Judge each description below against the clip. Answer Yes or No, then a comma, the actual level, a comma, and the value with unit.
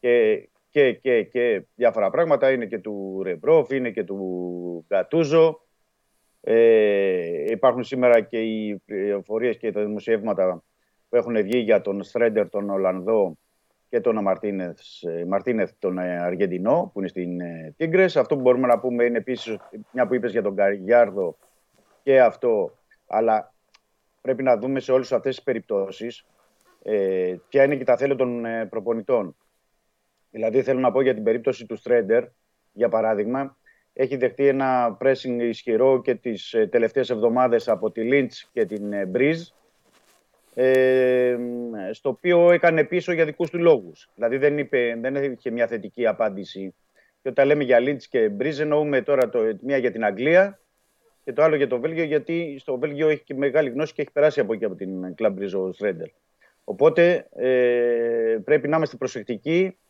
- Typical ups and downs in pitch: No, wide, 5.8 semitones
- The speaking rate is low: No, average, 155 wpm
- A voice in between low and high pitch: No, low, 130 Hz